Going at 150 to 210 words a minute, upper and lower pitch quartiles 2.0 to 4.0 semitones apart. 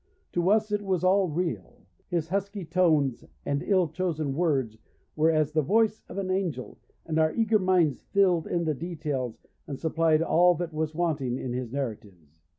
No: average, 175 wpm; average, 4.4 semitones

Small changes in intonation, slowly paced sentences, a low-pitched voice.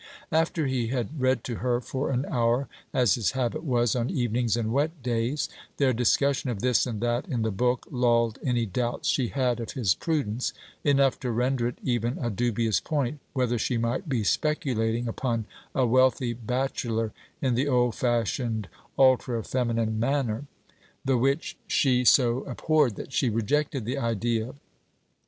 No: narrow, 2.2 semitones; average, 165 wpm; low, 125 Hz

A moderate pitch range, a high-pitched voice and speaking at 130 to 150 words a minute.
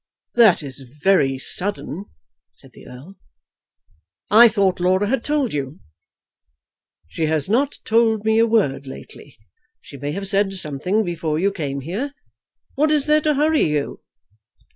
No: wide, 7.4 semitones; high, 195 Hz; average, 145 wpm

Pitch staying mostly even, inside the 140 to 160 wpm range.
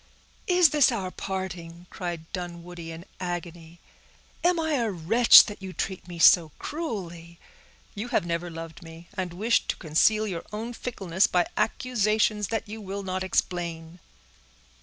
No: average, 4.1 semitones; average, 150 wpm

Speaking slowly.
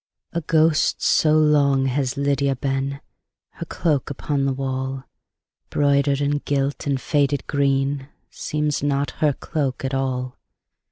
Yes: slow, 130 wpm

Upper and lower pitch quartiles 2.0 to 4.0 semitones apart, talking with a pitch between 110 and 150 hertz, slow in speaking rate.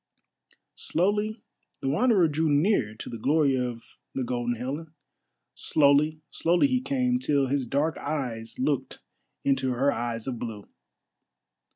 No: average, 4.7 semitones; medium, 140 Hz; slow, 130 wpm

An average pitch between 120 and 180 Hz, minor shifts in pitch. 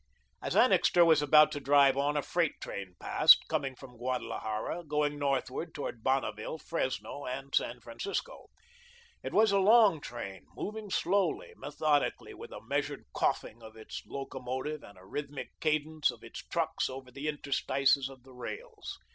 No: medium, 140 Hz; average, 3.4 semitones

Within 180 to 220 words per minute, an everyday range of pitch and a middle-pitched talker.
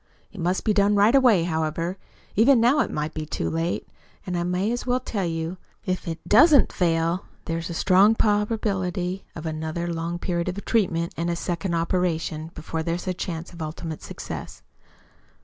Yes: average, 185 wpm; average, 3.5 semitones; medium, 175 Hz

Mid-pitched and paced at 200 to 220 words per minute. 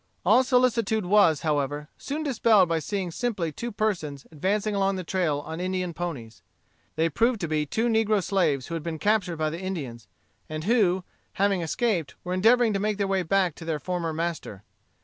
No: medium, 180 Hz; average, 190 wpm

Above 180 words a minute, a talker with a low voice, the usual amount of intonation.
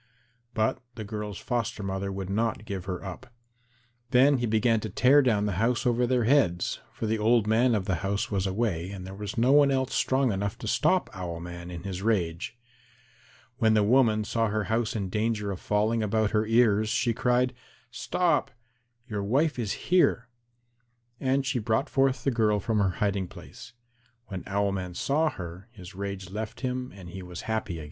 Yes: average, 190 wpm; low, 110 Hz; average, 3.8 semitones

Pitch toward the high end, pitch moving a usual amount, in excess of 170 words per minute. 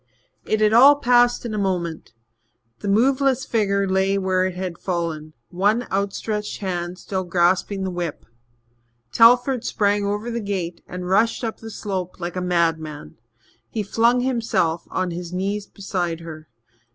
No: high, 195 Hz; average, 3.8 semitones; average, 150 wpm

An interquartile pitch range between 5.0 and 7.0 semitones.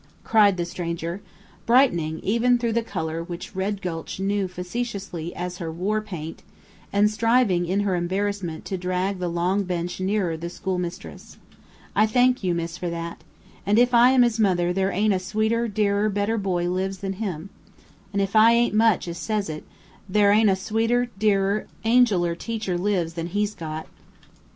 No: average, 3.6 semitones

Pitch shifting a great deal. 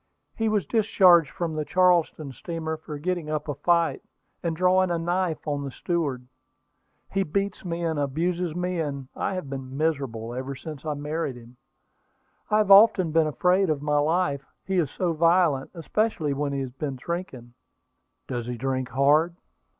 No: average, 4.2 semitones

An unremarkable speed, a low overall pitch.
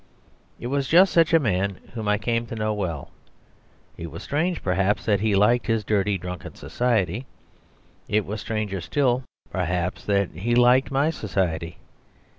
Yes: average, 160 wpm; low, 105 Hz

